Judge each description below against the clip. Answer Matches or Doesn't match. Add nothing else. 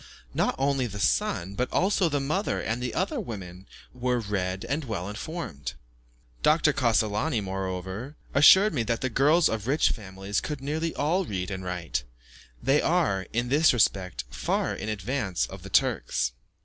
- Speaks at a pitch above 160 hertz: Doesn't match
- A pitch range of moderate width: Doesn't match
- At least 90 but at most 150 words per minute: Doesn't match